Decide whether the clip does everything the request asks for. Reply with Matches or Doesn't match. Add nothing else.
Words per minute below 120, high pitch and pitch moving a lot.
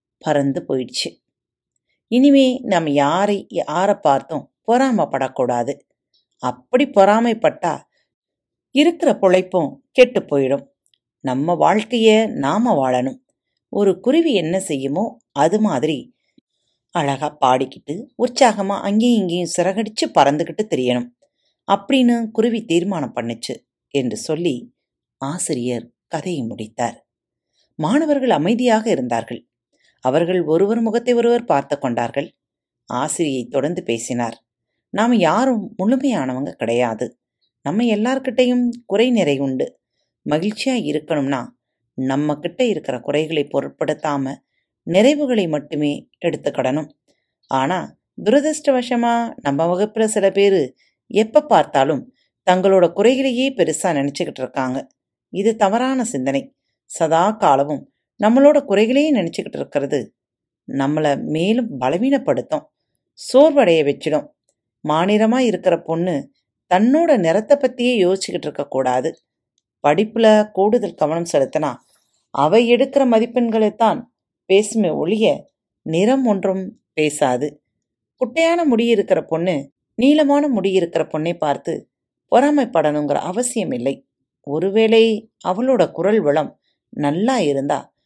Matches